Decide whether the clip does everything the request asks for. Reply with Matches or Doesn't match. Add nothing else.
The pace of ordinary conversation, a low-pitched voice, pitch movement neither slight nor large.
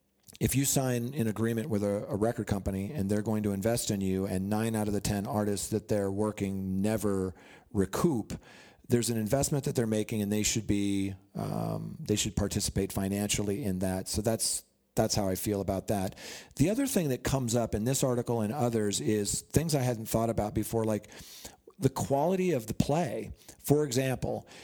Matches